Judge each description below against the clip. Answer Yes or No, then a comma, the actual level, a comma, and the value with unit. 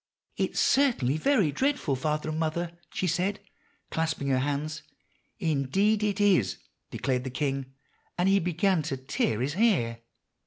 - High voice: No, medium, 155 Hz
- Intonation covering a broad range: Yes, wide, 6.1 semitones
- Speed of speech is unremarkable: Yes, average, 150 wpm